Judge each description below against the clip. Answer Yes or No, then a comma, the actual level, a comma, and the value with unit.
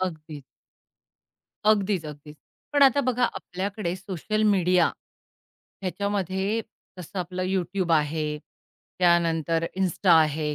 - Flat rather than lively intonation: No, average, 3.5 semitones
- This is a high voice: No, medium, 180 Hz